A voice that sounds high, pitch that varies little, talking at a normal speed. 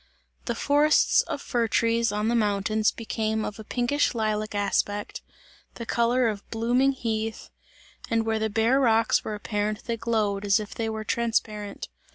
Yes: high, 225 Hz; narrow, 1.7 semitones; average, 165 wpm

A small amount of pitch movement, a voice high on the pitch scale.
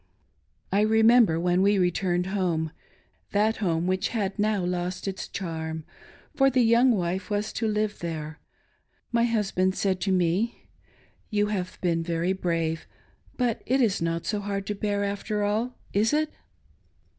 No: average, 3.5 semitones; high, 195 Hz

